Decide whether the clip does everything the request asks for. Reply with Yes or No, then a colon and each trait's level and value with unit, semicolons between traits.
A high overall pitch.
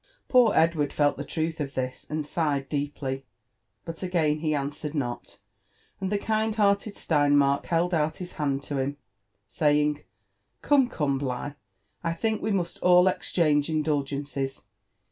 No: medium, 150 Hz